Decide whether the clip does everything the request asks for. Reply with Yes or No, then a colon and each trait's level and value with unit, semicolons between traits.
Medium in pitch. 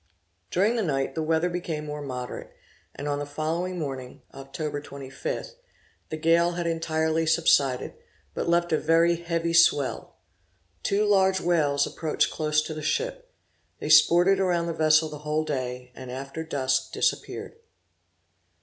Yes: medium, 155 Hz